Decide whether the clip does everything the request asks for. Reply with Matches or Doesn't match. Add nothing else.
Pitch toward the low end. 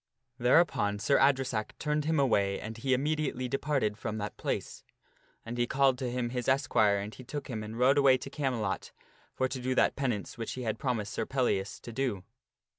Matches